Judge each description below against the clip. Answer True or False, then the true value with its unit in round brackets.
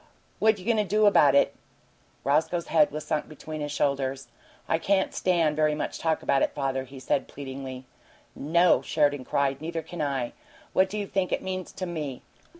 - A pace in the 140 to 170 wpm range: False (190 wpm)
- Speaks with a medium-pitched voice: True (155 Hz)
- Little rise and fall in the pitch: False (4.7 semitones)